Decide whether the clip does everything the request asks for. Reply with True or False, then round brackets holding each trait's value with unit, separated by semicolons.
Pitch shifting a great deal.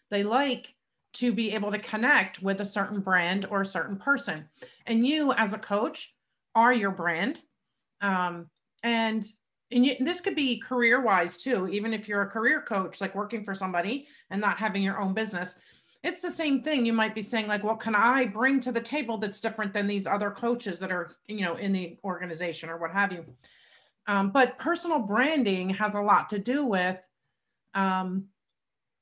False (4.0 semitones)